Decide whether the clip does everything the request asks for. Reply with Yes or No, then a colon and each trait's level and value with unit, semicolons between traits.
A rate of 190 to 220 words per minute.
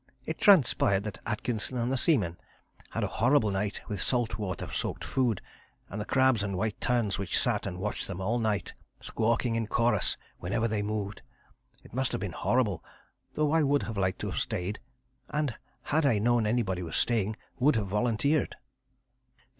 No: average, 175 wpm